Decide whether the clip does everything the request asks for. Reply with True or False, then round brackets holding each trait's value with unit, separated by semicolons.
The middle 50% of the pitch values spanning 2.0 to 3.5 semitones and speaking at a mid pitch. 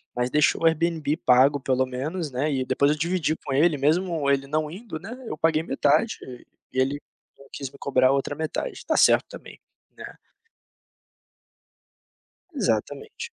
True (3.1 semitones; 150 Hz)